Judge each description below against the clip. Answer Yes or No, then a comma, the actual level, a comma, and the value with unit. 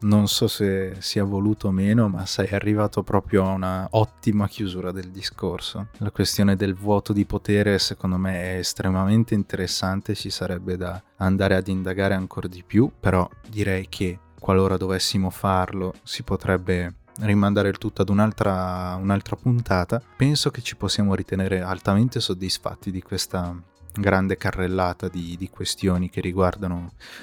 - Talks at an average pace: Yes, average, 150 wpm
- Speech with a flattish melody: Yes, narrow, 1.8 semitones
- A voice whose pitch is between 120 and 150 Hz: No, very low, 95 Hz